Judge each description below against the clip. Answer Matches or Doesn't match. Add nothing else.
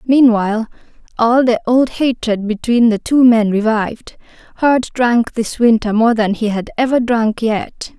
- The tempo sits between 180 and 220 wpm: Doesn't match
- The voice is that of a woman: Matches